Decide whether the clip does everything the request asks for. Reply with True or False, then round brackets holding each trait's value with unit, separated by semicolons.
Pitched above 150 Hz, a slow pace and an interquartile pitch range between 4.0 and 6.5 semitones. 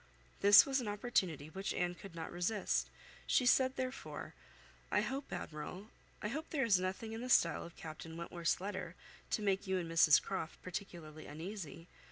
False (190 Hz; 175 wpm; 4.6 semitones)